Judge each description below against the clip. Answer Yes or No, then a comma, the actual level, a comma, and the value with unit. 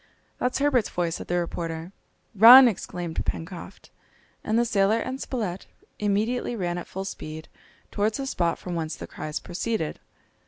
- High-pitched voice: Yes, high, 195 Hz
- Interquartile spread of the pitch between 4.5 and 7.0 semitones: Yes, average, 5.1 semitones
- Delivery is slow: No, average, 155 wpm